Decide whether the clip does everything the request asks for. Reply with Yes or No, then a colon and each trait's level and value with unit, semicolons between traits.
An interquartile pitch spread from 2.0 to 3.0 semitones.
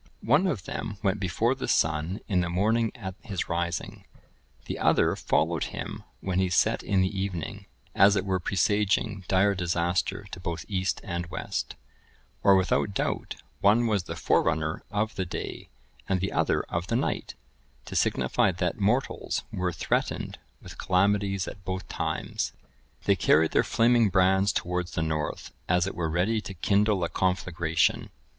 Yes: average, 2.7 semitones